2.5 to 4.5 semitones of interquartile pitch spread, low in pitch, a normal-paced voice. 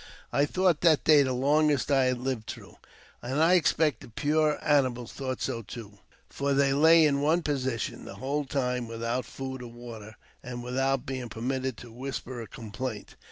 Yes: average, 3.2 semitones; low, 130 Hz; average, 180 wpm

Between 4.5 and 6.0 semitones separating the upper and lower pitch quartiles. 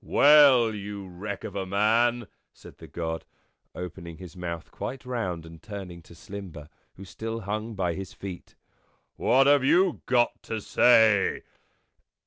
Yes: average, 4.9 semitones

